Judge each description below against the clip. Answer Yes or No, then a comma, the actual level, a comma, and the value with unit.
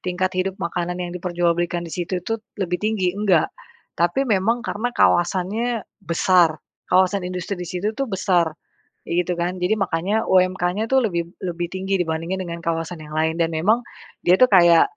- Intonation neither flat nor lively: No, narrow, 2.1 semitones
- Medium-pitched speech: Yes, medium, 180 Hz